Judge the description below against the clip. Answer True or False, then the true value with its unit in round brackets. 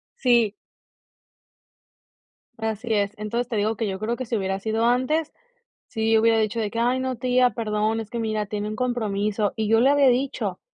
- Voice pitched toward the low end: False (225 Hz)